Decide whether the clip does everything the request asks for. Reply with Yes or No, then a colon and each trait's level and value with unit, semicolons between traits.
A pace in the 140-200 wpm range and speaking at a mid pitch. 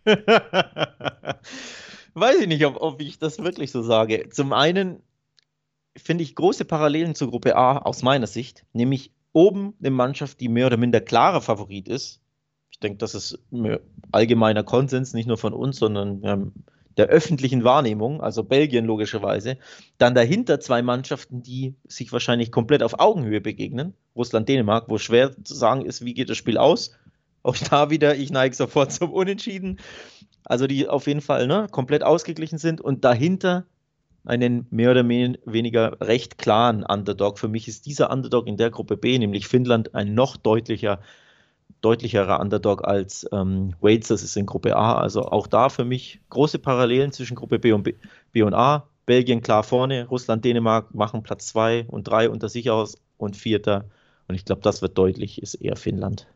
No: average, 170 wpm; low, 125 Hz